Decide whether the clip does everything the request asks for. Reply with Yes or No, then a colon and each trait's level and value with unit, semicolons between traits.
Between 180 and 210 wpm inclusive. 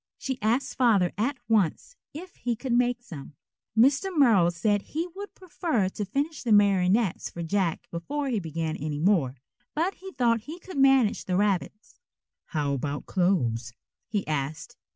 No: average, 160 wpm